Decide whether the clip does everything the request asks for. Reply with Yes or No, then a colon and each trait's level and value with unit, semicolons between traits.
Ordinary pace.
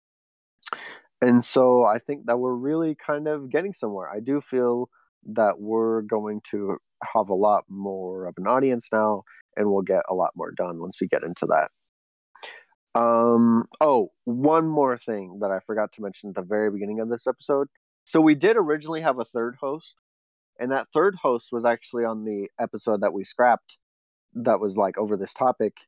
Yes: average, 190 wpm